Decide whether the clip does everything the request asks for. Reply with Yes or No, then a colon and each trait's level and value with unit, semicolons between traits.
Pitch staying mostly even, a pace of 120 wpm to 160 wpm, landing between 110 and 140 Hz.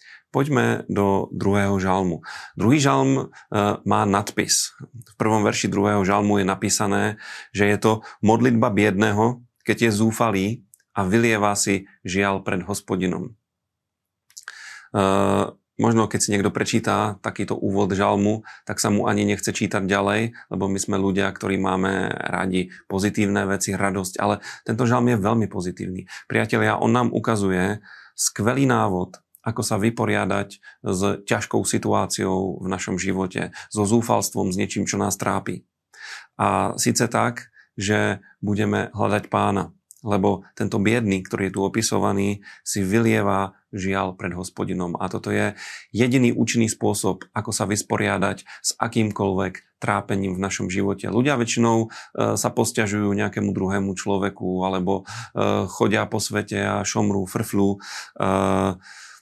No: narrow, 2.2 semitones; average, 135 wpm; low, 100 Hz